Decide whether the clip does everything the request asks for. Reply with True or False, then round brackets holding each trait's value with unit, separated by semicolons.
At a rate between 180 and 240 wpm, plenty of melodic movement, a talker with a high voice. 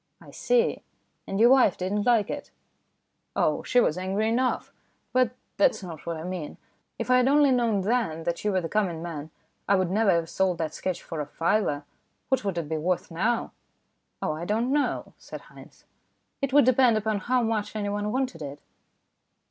True (205 wpm; 6.1 semitones; 205 Hz)